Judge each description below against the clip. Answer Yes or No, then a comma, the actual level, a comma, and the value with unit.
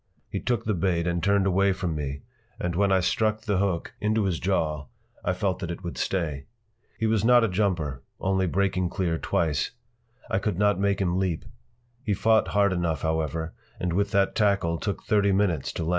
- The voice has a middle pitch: No, very low, 95 Hz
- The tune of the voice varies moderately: Yes, average, 3.1 semitones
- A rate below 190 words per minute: No, average, 195 wpm